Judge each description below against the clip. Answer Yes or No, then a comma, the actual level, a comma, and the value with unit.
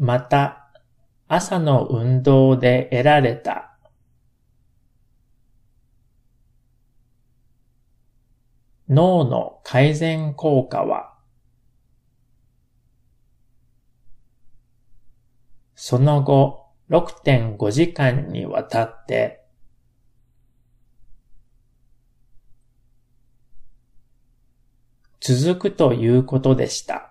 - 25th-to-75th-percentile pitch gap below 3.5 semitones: Yes, average, 2.7 semitones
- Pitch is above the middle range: No, low, 125 Hz